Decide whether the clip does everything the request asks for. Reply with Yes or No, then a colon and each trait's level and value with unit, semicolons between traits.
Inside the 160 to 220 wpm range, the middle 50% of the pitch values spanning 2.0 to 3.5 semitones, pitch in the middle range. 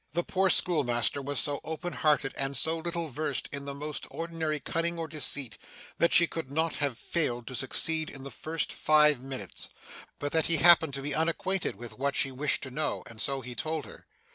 Yes: fast, 205 wpm; average, 3.1 semitones; medium, 150 Hz